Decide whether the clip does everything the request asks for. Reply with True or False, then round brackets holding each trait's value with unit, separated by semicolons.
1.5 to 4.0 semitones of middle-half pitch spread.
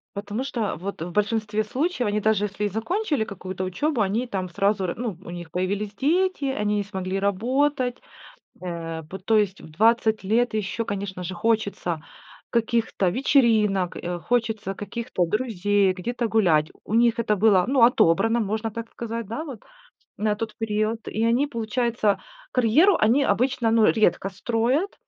True (3.4 semitones)